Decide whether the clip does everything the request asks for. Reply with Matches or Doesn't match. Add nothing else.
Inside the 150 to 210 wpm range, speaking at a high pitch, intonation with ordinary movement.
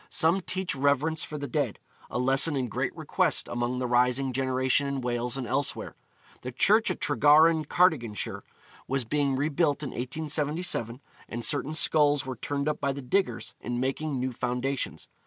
Doesn't match